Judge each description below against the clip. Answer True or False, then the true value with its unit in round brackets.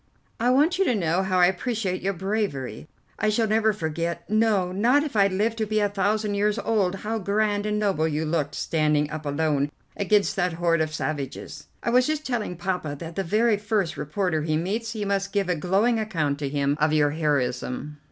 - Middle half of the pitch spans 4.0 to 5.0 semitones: False (5.4 semitones)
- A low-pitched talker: False (190 Hz)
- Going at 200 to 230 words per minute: True (205 wpm)